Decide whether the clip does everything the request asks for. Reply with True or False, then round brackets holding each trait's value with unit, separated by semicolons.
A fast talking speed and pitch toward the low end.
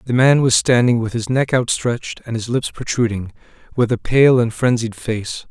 False (195 wpm; 120 Hz)